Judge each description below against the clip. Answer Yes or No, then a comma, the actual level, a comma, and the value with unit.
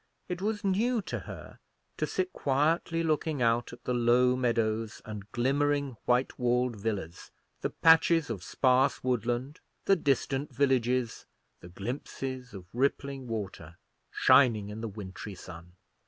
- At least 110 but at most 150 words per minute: Yes, average, 140 wpm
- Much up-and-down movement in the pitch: No, average, 4.2 semitones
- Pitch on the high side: No, low, 125 Hz